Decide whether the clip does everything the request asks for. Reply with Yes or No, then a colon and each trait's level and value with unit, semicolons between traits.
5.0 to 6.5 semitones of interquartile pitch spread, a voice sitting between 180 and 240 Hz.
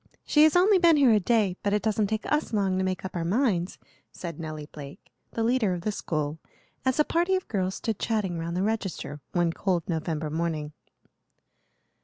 Yes: average, 5.3 semitones; high, 190 Hz